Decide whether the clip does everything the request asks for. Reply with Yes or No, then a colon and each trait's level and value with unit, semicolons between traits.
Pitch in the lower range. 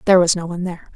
No: medium, 175 Hz